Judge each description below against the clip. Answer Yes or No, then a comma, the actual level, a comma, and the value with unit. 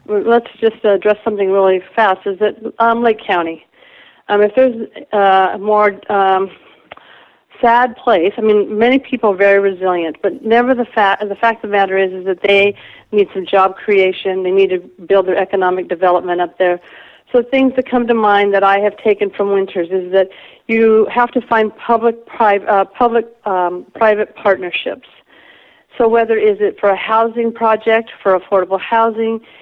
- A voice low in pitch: No, high, 205 Hz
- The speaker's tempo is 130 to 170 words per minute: No, average, 180 wpm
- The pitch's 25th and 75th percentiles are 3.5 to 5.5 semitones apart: No, average, 3.0 semitones